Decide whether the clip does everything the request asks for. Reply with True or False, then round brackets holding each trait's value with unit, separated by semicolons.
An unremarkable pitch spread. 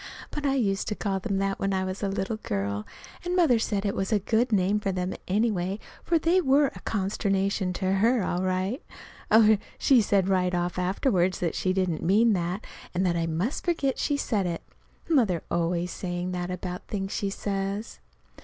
True (3.3 semitones)